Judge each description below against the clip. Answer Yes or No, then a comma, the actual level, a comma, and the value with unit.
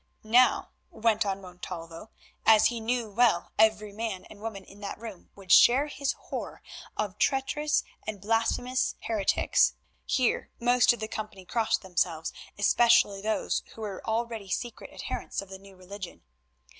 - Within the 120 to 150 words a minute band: Yes, average, 145 wpm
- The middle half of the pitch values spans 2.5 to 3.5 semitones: Yes, average, 3.2 semitones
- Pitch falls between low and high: No, high, 215 Hz